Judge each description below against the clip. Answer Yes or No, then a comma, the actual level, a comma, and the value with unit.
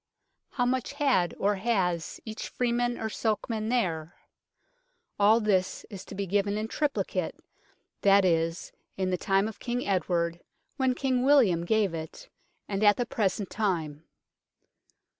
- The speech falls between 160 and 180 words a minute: No, average, 140 wpm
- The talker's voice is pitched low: No, high, 205 Hz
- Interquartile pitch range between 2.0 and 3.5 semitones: No, average, 4.6 semitones